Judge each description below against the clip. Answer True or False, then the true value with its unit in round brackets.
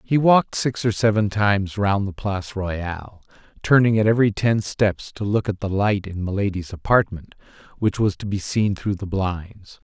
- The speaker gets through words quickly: False (190 wpm)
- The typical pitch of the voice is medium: False (100 Hz)